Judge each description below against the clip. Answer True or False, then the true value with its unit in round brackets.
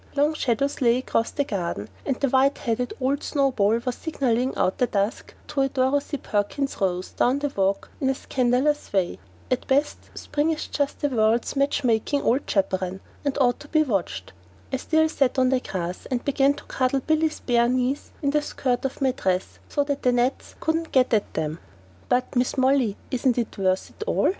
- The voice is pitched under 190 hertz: False (255 Hz)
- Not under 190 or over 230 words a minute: True (200 wpm)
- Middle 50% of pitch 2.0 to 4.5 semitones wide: True (3.8 semitones)